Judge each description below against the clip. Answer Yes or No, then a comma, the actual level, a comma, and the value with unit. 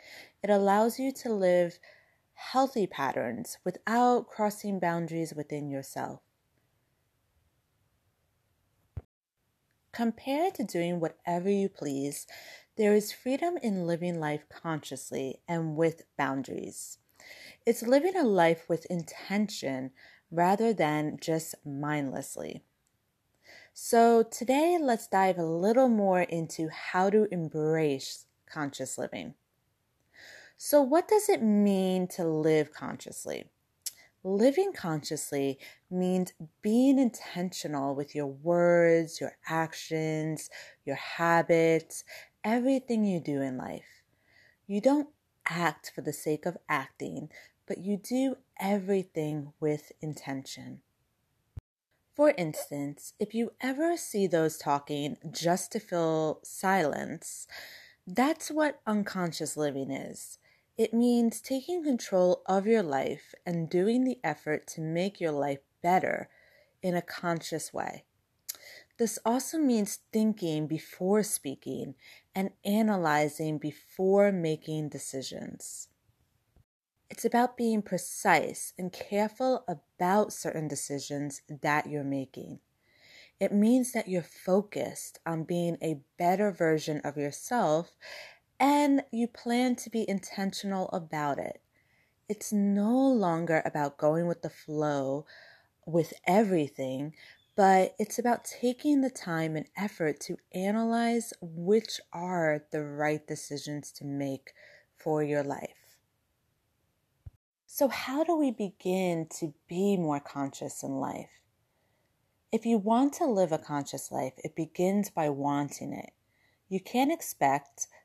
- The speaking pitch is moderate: Yes, medium, 175 Hz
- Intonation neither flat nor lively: No, wide, 6.2 semitones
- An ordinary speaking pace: No, slow, 115 wpm